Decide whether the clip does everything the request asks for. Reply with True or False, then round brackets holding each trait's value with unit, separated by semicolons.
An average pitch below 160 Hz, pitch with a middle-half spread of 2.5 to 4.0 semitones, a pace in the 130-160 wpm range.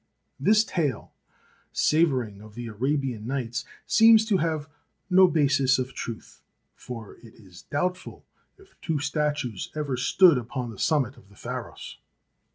False (135 Hz; 5.4 semitones; 145 wpm)